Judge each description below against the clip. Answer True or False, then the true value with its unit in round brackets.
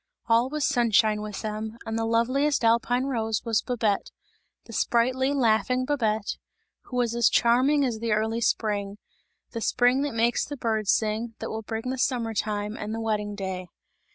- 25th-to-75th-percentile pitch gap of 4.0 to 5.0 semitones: False (2.4 semitones)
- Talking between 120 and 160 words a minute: False (175 wpm)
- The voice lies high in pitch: True (230 Hz)